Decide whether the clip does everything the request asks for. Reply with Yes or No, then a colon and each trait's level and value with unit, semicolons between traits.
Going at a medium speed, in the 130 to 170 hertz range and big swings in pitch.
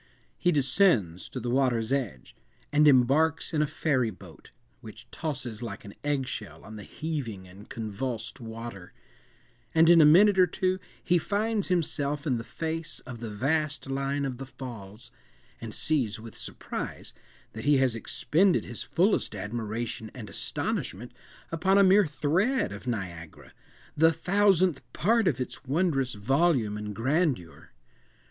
Yes: average, 150 wpm; low, 135 Hz; wide, 6.4 semitones